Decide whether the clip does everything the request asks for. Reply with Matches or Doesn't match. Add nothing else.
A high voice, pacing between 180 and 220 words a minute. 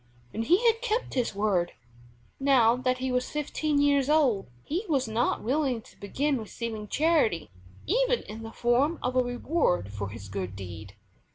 Doesn't match